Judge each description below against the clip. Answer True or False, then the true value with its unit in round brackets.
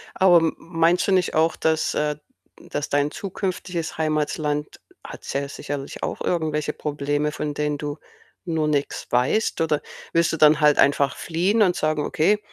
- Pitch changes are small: True (2.1 semitones)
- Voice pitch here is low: False (155 Hz)